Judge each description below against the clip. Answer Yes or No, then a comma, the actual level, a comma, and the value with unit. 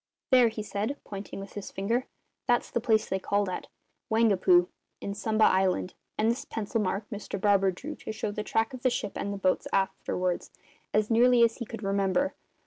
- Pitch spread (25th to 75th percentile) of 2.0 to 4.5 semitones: Yes, average, 2.7 semitones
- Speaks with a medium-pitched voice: No, high, 210 Hz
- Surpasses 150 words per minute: Yes, average, 195 wpm